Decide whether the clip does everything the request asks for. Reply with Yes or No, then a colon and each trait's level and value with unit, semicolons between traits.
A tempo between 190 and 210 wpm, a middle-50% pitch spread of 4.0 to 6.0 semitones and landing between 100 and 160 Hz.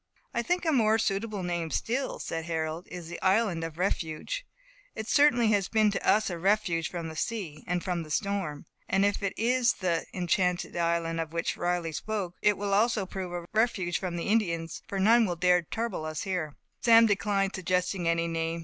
No: average, 200 wpm; average, 4.3 semitones; medium, 185 Hz